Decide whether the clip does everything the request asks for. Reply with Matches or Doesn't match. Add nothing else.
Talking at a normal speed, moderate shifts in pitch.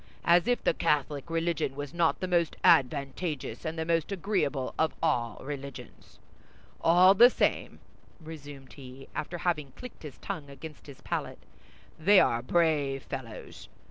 Matches